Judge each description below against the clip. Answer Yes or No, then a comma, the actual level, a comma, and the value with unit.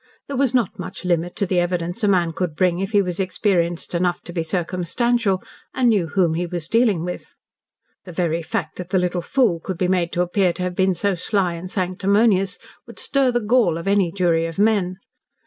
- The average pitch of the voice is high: No, medium, 180 Hz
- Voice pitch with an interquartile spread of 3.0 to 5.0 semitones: No, narrow, 2.6 semitones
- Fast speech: Yes, fast, 215 wpm